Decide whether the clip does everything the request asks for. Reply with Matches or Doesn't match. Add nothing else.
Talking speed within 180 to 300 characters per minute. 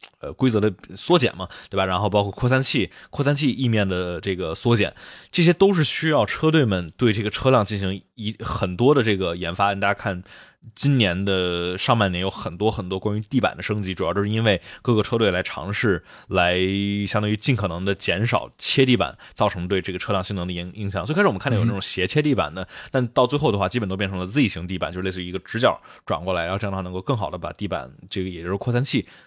Doesn't match